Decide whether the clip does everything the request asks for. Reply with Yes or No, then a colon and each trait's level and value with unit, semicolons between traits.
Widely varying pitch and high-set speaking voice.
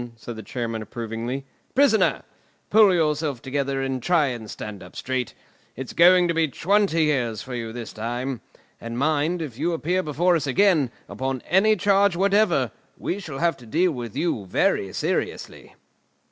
No: wide, 6.5 semitones; medium, 140 Hz